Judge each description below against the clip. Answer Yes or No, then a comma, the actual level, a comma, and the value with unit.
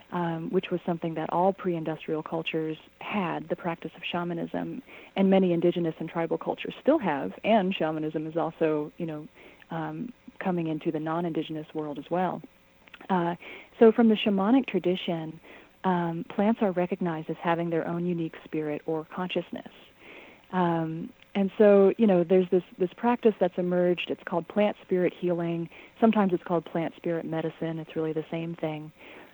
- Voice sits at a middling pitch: Yes, medium, 170 Hz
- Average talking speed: Yes, average, 165 wpm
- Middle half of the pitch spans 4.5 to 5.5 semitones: No, narrow, 2.6 semitones